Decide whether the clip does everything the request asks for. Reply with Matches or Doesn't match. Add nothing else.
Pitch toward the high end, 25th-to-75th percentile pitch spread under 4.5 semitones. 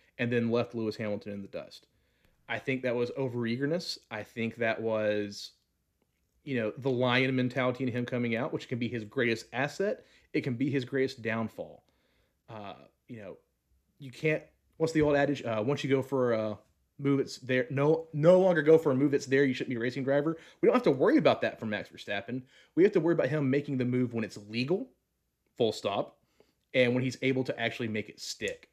Doesn't match